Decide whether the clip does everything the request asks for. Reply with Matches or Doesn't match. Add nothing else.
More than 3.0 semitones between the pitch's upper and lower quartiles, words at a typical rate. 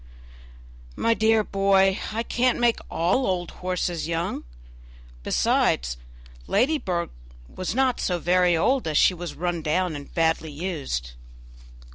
Doesn't match